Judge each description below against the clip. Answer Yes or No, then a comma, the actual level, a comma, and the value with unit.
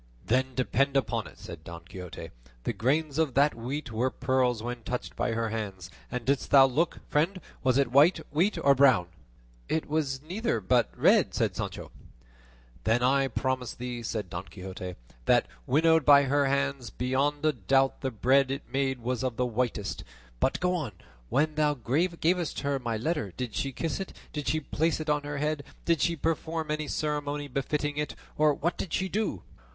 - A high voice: No, low, 135 Hz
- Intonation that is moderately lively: Yes, average, 3.9 semitones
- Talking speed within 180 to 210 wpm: Yes, average, 185 wpm